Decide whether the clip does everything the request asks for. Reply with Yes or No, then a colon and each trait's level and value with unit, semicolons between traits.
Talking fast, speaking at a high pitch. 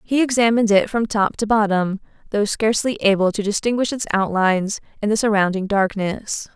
No: average, 165 wpm; high, 210 Hz